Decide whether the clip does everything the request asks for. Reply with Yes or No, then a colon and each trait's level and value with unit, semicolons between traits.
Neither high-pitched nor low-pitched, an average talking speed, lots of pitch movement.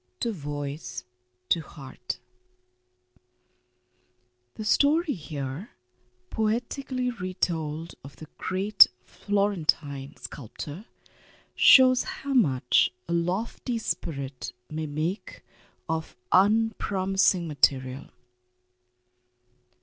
No: medium, 170 Hz; slow, 75 wpm; wide, 6.8 semitones